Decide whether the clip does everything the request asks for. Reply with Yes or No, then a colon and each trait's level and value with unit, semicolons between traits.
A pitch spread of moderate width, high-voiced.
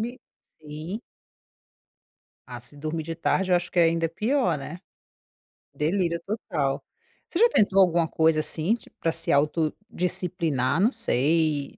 No: average, 3.7 semitones; medium, 165 Hz